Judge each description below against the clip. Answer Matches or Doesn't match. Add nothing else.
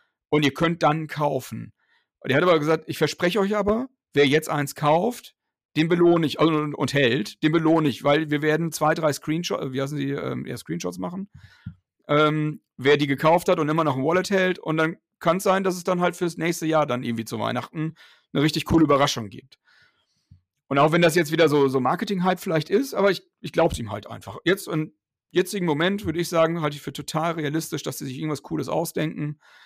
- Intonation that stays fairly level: Doesn't match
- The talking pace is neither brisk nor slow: Doesn't match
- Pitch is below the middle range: Doesn't match